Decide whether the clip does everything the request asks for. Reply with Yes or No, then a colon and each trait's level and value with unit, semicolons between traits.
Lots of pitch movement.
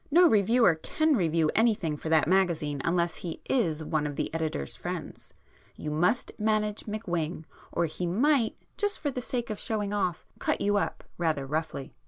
Yes: wide, 5.7 semitones